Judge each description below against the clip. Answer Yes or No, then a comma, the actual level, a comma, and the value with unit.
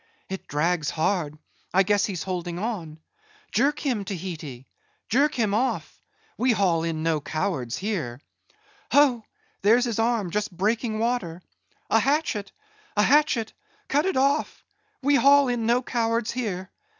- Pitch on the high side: Yes, high, 210 Hz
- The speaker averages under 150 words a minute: Yes, average, 140 wpm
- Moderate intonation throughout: No, wide, 6.0 semitones